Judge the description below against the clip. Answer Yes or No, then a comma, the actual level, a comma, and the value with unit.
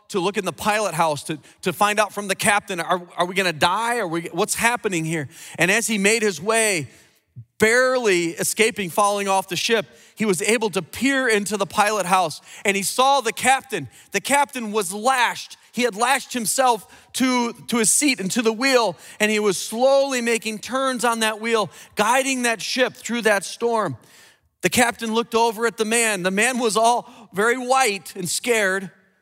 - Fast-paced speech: No, average, 195 wpm